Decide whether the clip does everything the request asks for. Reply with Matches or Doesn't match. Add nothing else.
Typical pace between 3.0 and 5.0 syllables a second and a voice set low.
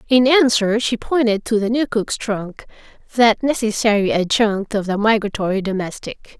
Doesn't match